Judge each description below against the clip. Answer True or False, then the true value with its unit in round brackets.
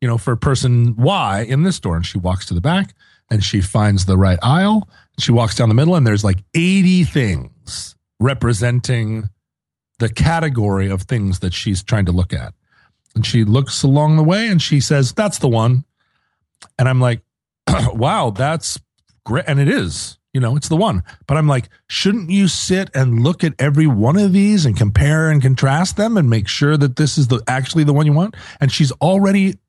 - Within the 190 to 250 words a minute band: True (200 wpm)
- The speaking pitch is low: True (130 Hz)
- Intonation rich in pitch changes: True (6.3 semitones)